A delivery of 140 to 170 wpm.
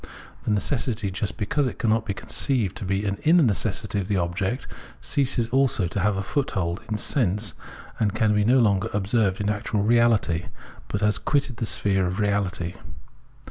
No: average, 180 wpm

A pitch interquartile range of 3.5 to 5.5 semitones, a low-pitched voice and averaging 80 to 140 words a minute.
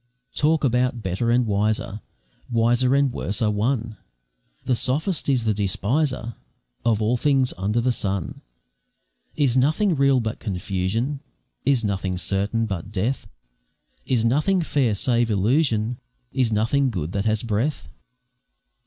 Yes: average, 4.1 semitones; low, 115 Hz; slow, 135 wpm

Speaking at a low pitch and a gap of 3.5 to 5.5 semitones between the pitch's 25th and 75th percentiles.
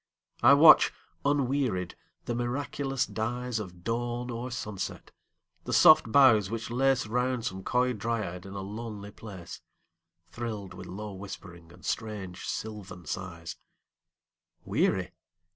Yes: low, 110 Hz; average, 4.4 semitones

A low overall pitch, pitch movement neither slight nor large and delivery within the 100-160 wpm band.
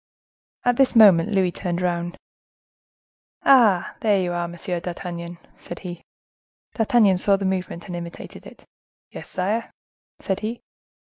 No: medium, 185 Hz; average, 3.2 semitones; slow, 135 wpm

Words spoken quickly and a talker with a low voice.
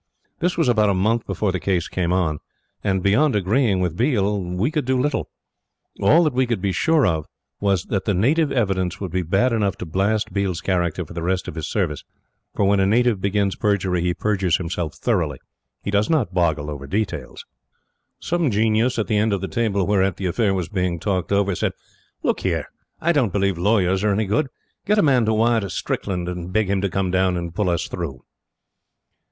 Yes: fast, 210 wpm; low, 100 Hz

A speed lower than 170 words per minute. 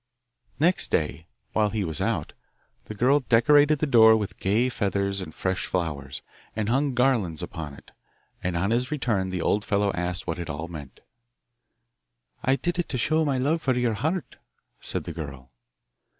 No: average, 175 wpm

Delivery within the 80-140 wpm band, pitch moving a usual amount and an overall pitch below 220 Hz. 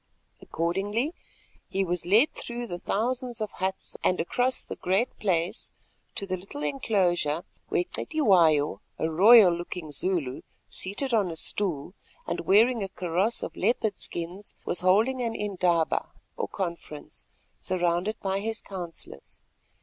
Yes: slow, 135 wpm; average, 4.1 semitones; high, 190 Hz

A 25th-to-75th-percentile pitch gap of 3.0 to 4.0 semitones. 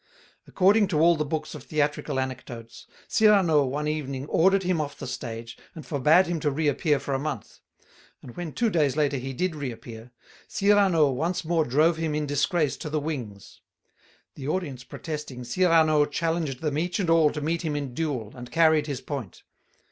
Yes: average, 3.5 semitones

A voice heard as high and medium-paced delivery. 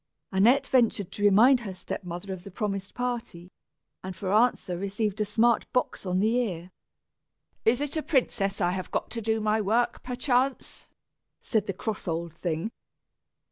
Yes: high, 210 Hz; average, 170 wpm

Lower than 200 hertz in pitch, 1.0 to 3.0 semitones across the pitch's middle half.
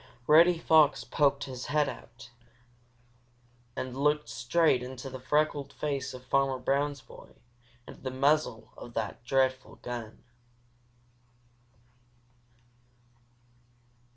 Yes: low, 135 Hz; average, 2.7 semitones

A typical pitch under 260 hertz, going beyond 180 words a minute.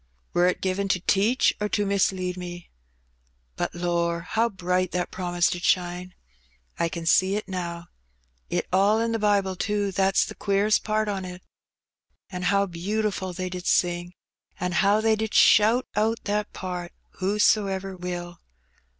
No: high, 190 Hz; average, 160 wpm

